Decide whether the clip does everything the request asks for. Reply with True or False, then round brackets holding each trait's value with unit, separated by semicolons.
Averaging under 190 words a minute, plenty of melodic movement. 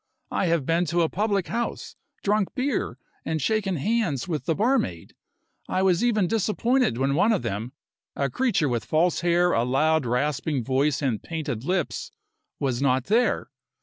True (165 wpm; 7.2 semitones)